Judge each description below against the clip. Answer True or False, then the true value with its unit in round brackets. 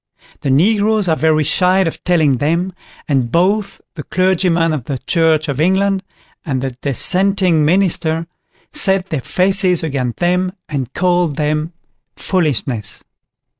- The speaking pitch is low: False (165 Hz)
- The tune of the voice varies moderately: True (4.0 semitones)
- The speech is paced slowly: True (130 wpm)